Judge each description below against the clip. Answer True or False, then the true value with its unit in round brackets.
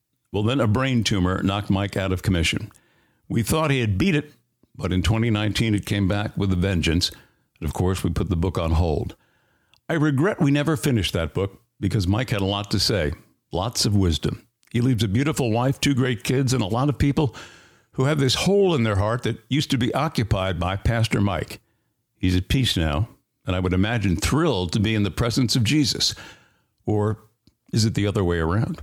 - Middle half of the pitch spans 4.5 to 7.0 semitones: True (5.1 semitones)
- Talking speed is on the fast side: True (210 wpm)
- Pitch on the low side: True (110 Hz)